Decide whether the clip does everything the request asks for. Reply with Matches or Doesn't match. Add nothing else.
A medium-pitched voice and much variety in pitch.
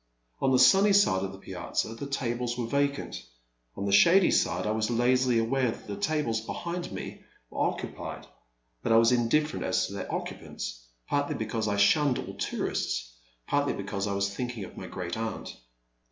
Doesn't match